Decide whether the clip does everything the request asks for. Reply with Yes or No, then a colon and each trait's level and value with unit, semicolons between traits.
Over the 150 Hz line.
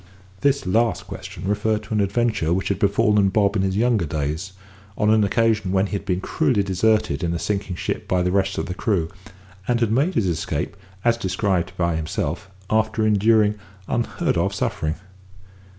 No: low, 100 Hz